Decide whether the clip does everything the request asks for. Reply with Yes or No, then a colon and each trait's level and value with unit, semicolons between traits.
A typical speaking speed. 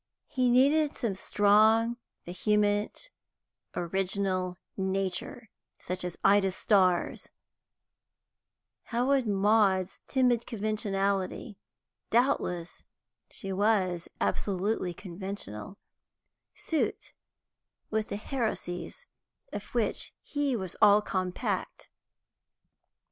No: slow, 80 wpm